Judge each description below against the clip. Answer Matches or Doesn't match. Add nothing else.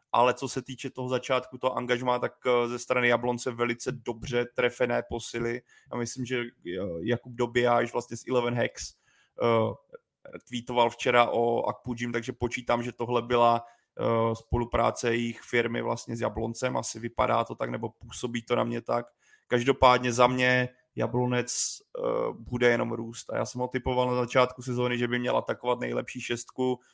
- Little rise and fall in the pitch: Matches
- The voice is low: Matches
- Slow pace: Doesn't match